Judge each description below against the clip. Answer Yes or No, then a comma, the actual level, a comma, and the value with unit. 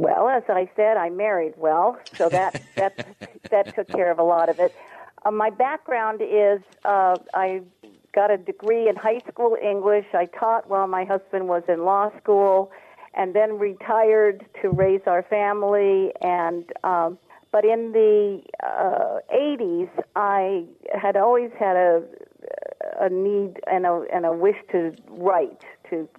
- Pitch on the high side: Yes, high, 200 Hz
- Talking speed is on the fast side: No, average, 160 wpm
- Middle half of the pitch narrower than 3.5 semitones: Yes, average, 2.8 semitones